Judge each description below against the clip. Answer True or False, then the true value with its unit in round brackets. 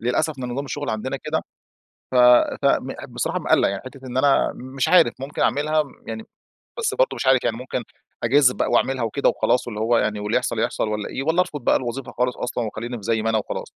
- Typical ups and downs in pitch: True (3.6 semitones)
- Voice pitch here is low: True (125 Hz)